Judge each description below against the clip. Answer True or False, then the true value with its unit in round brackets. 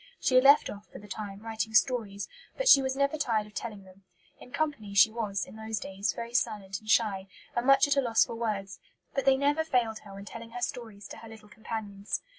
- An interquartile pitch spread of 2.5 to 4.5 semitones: True (3.7 semitones)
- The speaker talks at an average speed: False (230 wpm)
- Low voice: False (220 Hz)